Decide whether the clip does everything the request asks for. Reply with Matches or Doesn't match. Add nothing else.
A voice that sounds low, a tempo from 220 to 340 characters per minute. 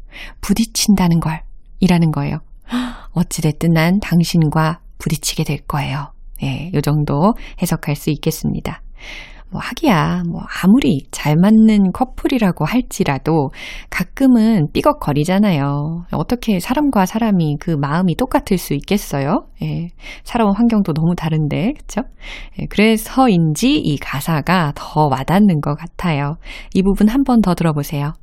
Doesn't match